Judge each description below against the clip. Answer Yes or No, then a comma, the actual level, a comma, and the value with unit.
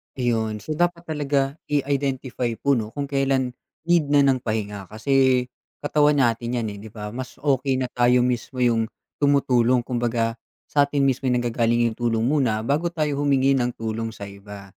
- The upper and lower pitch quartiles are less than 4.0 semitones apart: Yes, average, 3.6 semitones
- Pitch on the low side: Yes, low, 125 Hz